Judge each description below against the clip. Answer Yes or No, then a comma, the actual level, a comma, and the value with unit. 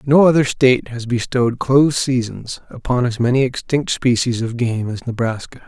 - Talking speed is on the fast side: No, average, 170 wpm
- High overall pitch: No, low, 125 Hz